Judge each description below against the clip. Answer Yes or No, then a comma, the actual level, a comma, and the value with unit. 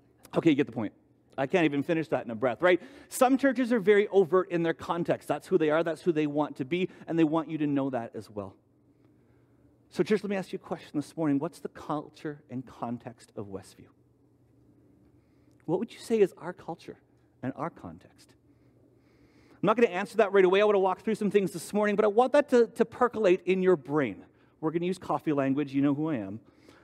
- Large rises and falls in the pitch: Yes, wide, 6.0 semitones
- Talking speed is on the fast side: Yes, fast, 235 wpm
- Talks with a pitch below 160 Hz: No, medium, 170 Hz